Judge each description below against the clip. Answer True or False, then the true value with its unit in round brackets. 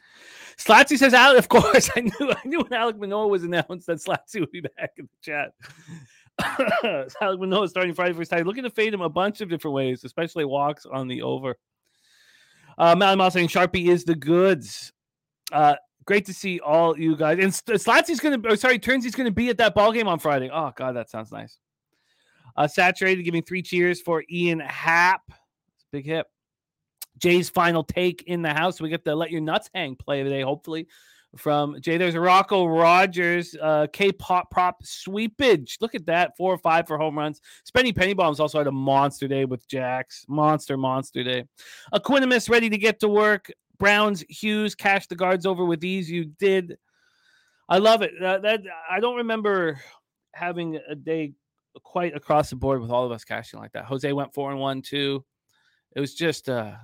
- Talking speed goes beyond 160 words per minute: True (195 wpm)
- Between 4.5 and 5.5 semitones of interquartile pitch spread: True (5.0 semitones)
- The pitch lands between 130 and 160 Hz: False (175 Hz)